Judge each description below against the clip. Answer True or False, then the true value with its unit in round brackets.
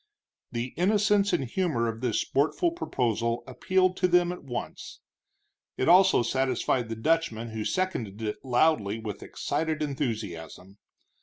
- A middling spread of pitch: False (7.6 semitones)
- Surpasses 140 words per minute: False (135 wpm)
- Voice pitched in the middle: False (130 Hz)